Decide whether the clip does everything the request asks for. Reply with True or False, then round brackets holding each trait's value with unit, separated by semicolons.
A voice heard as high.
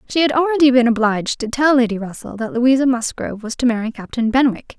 True (245 Hz)